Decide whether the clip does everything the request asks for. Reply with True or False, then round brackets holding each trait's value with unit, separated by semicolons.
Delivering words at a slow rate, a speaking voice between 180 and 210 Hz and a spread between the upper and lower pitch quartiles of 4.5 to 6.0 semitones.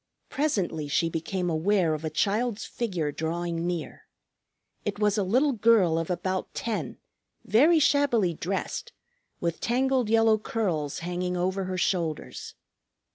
True (130 wpm; 185 Hz; 5.1 semitones)